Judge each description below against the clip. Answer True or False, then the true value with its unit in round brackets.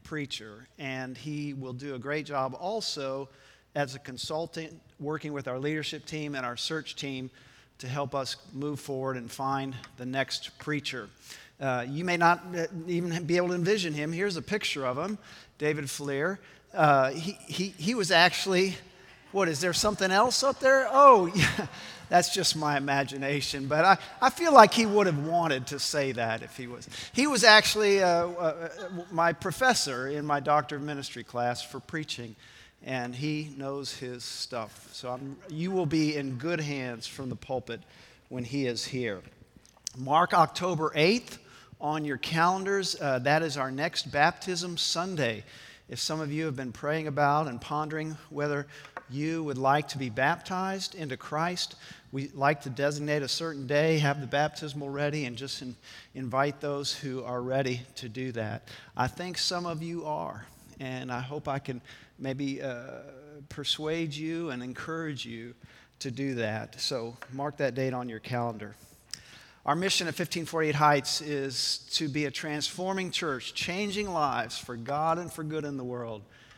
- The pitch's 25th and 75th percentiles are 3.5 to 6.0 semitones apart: True (4.1 semitones)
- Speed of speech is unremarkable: True (170 wpm)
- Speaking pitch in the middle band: True (145 Hz)